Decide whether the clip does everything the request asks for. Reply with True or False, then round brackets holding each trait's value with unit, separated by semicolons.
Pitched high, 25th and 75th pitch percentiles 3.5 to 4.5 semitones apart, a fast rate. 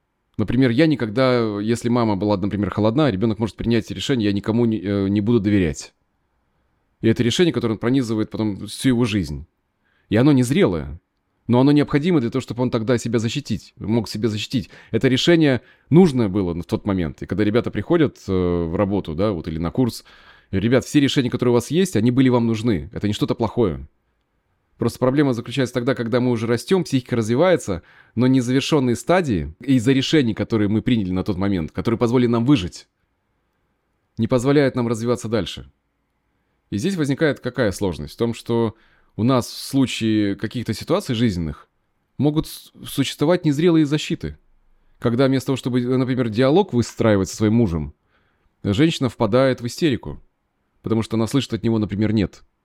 False (115 Hz; 4.1 semitones; 170 wpm)